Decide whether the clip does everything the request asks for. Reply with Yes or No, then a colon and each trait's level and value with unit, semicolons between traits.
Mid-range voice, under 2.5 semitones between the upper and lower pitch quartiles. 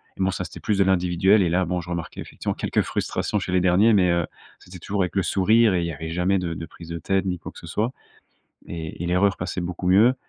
No: very low, 90 Hz; narrow, 2.0 semitones